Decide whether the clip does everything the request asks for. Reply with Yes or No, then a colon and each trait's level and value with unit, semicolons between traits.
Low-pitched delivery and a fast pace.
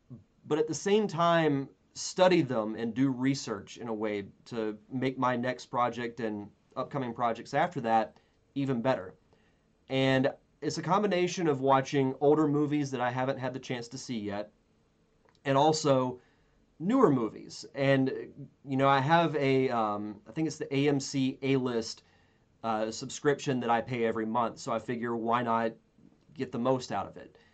No: low, 130 Hz; average, 170 wpm